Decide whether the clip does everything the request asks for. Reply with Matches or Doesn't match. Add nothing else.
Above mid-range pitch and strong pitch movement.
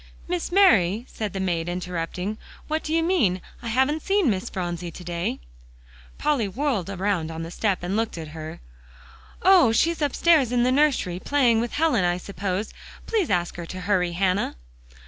Matches